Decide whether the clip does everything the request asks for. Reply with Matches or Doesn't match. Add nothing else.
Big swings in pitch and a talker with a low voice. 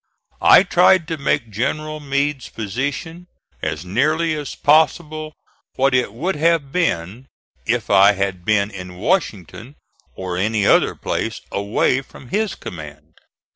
Matches